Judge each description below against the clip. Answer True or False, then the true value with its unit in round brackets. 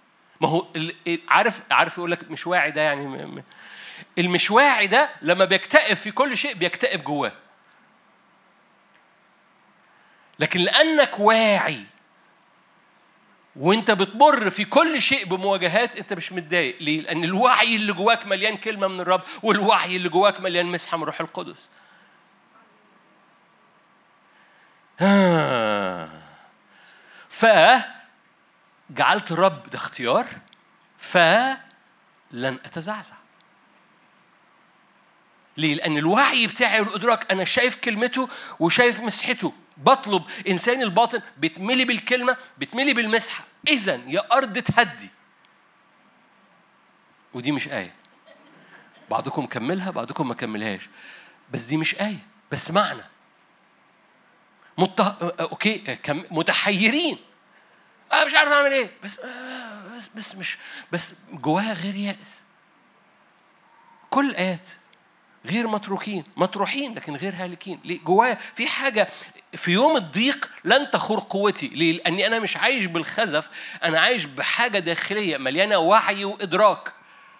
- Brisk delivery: False (105 wpm)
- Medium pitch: False (200 Hz)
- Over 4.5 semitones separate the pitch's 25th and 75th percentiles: True (5.5 semitones)